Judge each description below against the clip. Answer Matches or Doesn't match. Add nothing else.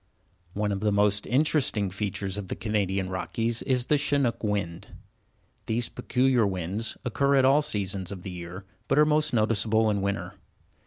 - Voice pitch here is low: Matches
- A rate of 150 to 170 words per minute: Matches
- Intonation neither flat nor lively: Matches